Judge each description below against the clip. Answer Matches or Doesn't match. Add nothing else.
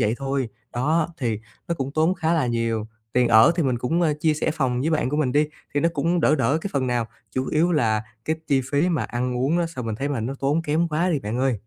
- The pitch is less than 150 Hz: Matches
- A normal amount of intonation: Matches